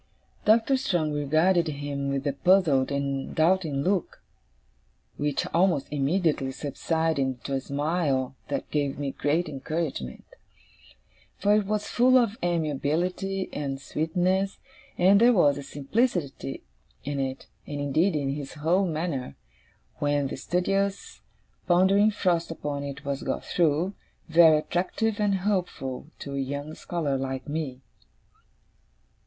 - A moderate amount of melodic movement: Yes, average, 4.7 semitones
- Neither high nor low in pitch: Yes, medium, 155 Hz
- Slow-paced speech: Yes, slow, 130 wpm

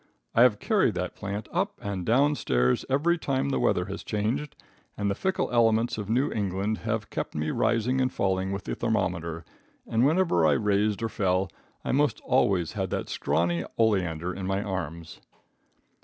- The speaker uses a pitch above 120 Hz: No, low, 105 Hz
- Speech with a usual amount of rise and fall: Yes, average, 4.8 semitones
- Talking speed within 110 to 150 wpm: No, average, 175 wpm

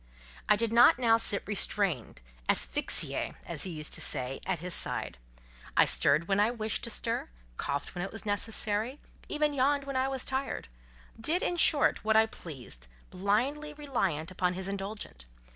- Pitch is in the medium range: No, high, 205 Hz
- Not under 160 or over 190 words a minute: Yes, average, 165 wpm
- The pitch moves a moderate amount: No, wide, 7.3 semitones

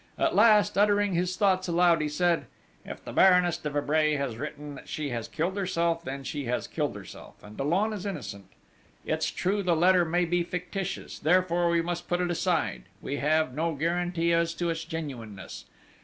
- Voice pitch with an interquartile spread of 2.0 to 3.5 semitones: Yes, average, 3.1 semitones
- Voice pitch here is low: No, medium, 170 Hz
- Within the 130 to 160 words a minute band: No, average, 185 wpm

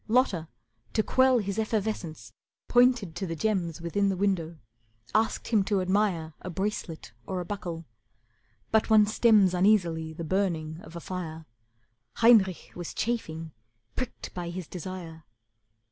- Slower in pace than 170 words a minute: Yes, average, 140 wpm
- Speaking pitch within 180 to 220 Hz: Yes, medium, 185 Hz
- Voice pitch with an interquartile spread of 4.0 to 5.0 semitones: Yes, average, 4.4 semitones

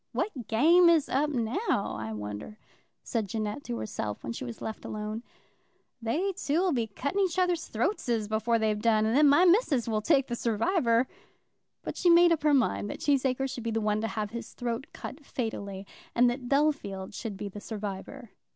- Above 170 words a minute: Yes, average, 190 wpm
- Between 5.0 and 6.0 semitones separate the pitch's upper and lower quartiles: Yes, wide, 5.5 semitones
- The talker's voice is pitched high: Yes, high, 235 Hz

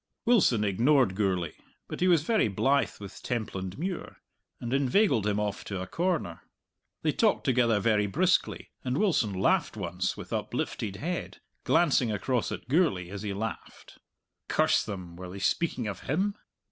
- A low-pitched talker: Yes, low, 115 Hz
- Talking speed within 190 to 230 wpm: No, average, 155 wpm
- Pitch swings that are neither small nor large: No, wide, 7.9 semitones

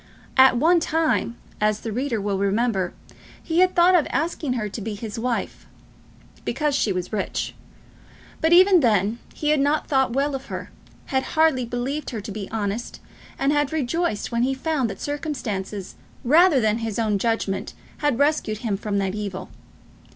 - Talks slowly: No, average, 175 wpm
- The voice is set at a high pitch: Yes, high, 245 Hz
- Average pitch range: No, wide, 5.7 semitones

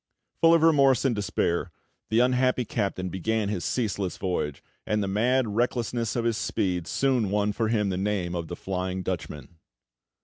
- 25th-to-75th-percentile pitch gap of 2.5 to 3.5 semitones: No, average, 4.6 semitones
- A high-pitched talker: No, low, 105 Hz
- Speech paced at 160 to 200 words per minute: Yes, average, 170 wpm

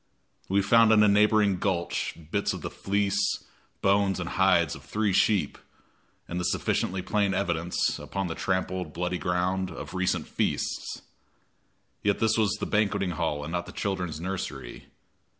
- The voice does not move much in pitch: Yes, narrow, 2.3 semitones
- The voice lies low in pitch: Yes, very low, 95 Hz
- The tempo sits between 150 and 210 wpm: Yes, average, 160 wpm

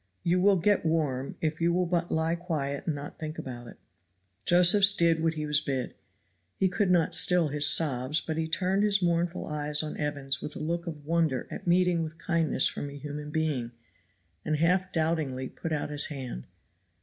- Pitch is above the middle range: No, medium, 160 Hz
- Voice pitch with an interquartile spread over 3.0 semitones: No, average, 2.7 semitones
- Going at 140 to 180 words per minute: No, average, 195 wpm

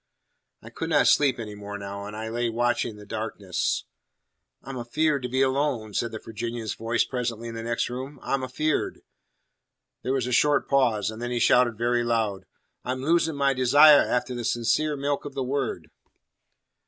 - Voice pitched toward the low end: Yes, low, 120 Hz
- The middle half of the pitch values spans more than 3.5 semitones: No, average, 3.2 semitones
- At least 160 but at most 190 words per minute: Yes, average, 180 wpm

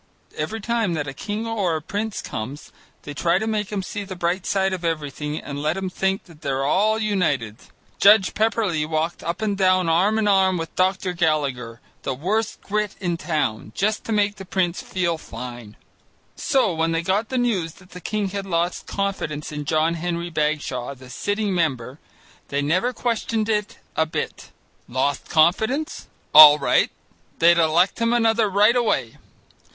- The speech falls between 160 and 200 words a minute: Yes, average, 175 wpm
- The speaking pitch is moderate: Yes, medium, 180 Hz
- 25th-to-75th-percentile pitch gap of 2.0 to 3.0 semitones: No, average, 5.2 semitones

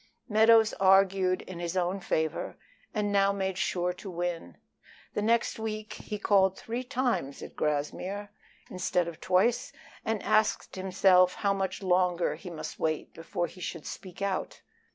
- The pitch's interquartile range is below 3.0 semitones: Yes, narrow, 2.6 semitones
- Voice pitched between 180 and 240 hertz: Yes, high, 190 Hz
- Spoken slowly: No, average, 155 wpm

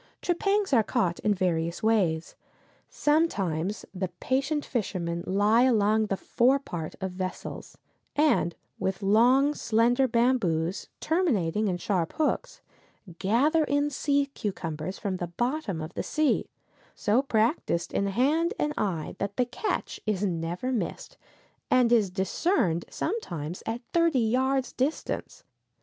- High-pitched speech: Yes, high, 220 Hz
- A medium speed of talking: No, slow, 130 wpm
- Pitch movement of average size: No, wide, 6.9 semitones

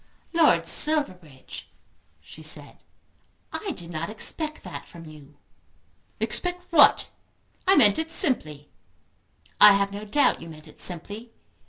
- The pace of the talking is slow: Yes, slow, 130 wpm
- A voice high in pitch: Yes, high, 200 Hz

